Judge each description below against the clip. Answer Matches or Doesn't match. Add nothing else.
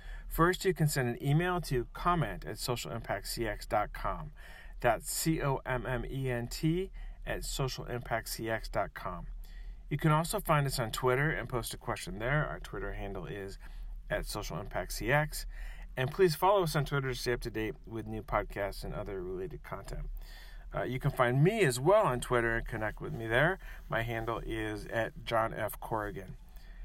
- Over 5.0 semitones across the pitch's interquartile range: Matches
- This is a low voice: Matches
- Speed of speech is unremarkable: Matches